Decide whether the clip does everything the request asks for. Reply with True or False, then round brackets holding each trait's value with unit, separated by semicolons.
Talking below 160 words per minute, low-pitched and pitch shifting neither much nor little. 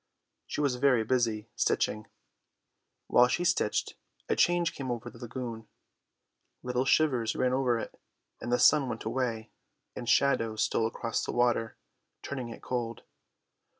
False (145 wpm; 120 Hz; 2.3 semitones)